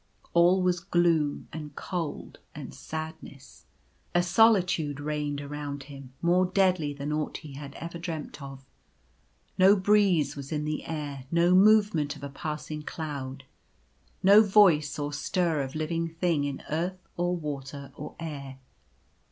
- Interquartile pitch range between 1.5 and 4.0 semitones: Yes, average, 3.6 semitones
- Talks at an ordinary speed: Yes, average, 145 wpm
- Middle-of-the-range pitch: Yes, medium, 155 Hz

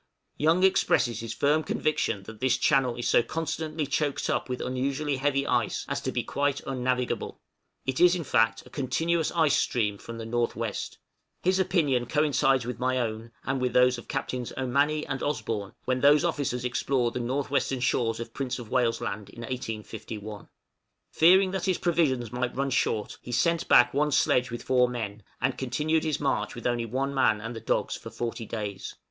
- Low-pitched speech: Yes, low, 130 Hz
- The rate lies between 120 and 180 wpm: No, average, 190 wpm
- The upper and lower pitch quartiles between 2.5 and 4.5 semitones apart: Yes, average, 3.7 semitones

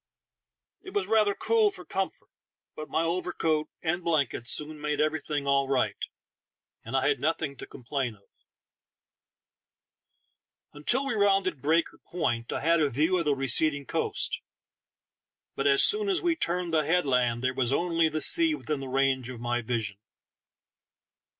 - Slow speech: No, average, 155 wpm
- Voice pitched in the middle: Yes, medium, 150 Hz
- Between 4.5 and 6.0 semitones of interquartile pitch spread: Yes, average, 5.0 semitones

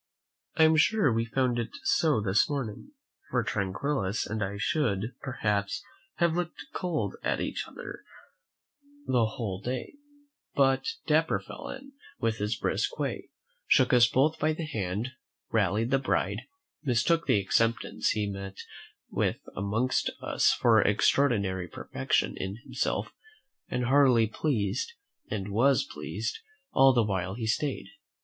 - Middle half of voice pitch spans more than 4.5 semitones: Yes, average, 5.1 semitones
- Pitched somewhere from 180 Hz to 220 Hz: No, low, 115 Hz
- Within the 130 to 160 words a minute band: Yes, average, 140 wpm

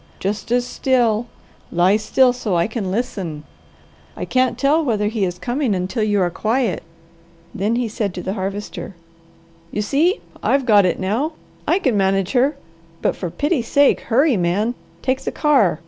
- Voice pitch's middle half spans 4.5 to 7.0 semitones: Yes, average, 5.0 semitones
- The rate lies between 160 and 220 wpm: Yes, average, 170 wpm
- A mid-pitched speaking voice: No, high, 220 Hz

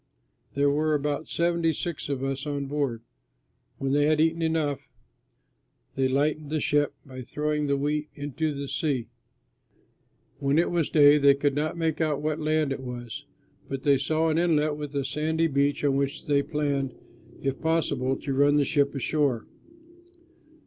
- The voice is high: No, medium, 145 Hz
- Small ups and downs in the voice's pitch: Yes, narrow, 1.9 semitones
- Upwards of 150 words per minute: Yes, average, 170 wpm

